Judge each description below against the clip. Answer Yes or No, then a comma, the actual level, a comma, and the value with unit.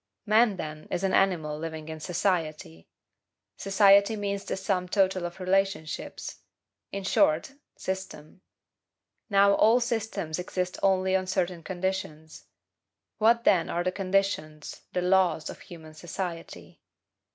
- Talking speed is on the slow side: Yes, slow, 125 wpm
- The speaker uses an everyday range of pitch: Yes, average, 3.2 semitones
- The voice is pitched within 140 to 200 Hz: Yes, medium, 185 Hz